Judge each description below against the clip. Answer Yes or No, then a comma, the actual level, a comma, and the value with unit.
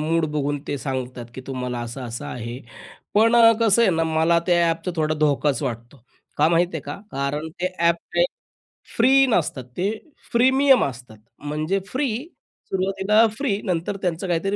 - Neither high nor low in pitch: Yes, medium, 165 Hz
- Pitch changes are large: Yes, wide, 6.0 semitones